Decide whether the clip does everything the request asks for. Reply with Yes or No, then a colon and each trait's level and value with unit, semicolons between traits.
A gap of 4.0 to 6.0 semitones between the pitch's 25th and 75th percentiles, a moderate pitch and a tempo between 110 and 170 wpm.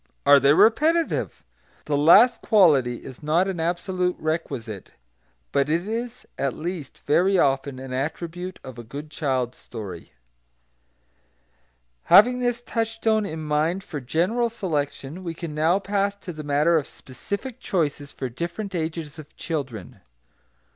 Yes: wide, 5.5 semitones; medium, 160 Hz; average, 140 wpm